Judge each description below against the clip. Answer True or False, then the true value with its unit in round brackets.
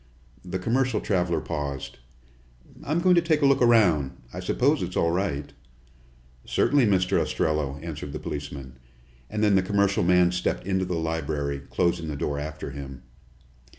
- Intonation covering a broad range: True (5.7 semitones)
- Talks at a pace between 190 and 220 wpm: False (155 wpm)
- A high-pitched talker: False (85 Hz)